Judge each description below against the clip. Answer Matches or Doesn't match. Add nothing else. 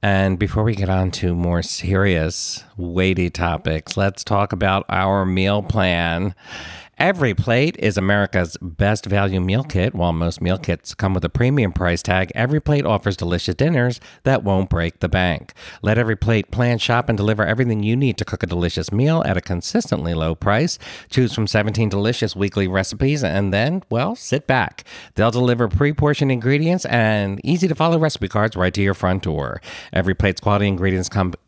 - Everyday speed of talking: Matches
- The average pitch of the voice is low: Matches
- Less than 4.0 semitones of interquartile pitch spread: Doesn't match